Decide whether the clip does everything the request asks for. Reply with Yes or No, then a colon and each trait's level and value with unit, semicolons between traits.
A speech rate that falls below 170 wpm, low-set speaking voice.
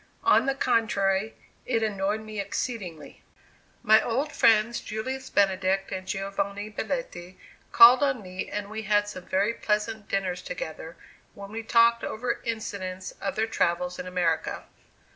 No: average, 145 wpm; high, 210 Hz